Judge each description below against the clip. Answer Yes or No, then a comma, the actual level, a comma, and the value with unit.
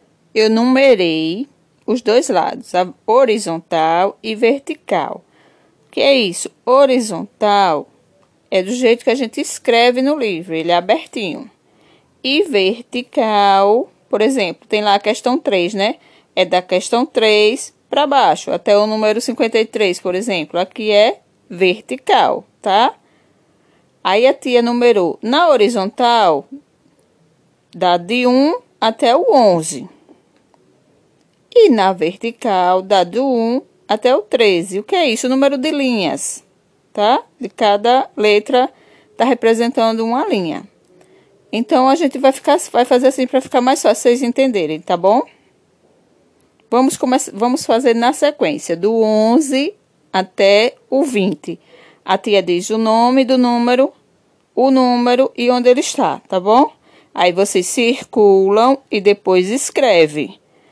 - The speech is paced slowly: No, average, 135 wpm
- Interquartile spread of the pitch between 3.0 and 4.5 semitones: No, average, 4.9 semitones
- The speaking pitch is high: Yes, high, 235 Hz